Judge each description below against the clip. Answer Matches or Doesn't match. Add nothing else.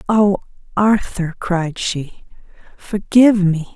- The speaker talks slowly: Matches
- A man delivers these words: Doesn't match